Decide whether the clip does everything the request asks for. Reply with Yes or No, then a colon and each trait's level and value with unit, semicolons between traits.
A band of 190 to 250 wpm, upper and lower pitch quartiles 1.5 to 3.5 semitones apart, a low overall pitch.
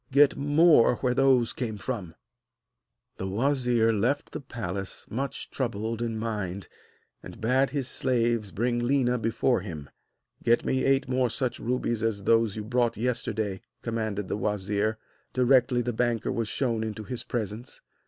No: average, 150 wpm; average, 2.8 semitones; low, 115 Hz